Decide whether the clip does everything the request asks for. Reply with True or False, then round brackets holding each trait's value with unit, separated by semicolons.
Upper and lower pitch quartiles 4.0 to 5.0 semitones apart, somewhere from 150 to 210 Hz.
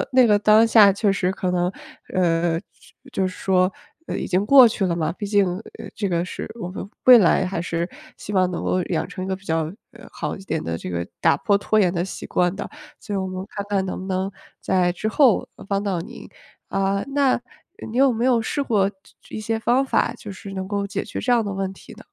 False (2.8 semitones; 195 Hz)